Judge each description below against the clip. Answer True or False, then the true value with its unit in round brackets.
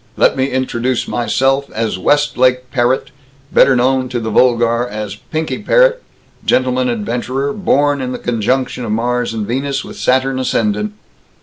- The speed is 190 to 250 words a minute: False (145 wpm)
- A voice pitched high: False (125 Hz)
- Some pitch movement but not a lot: False (2.2 semitones)